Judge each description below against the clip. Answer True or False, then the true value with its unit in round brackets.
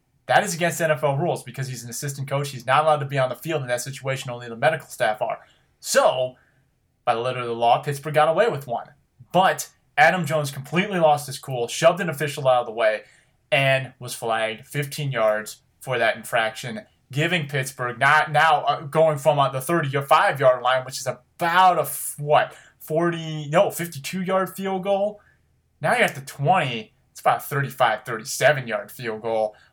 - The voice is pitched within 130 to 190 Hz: True (140 Hz)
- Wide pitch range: False (3.7 semitones)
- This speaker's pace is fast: False (190 wpm)